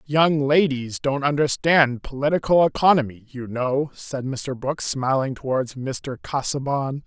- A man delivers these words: Yes, male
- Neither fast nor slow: No, slow, 125 wpm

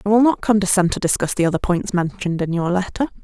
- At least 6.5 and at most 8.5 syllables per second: Yes, 6.7 syllables/s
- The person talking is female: Yes, female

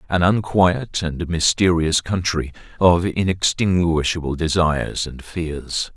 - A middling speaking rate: No, slow, 100 wpm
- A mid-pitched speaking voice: No, very low, 85 Hz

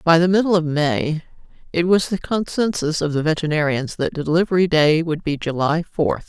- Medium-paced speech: Yes, average, 180 wpm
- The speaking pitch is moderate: Yes, medium, 160 Hz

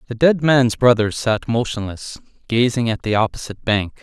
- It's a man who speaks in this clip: Yes, male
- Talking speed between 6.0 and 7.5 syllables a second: No, 5.0 syllables/s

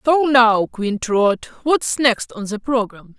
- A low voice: No, high, 235 Hz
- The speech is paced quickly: No, average, 170 wpm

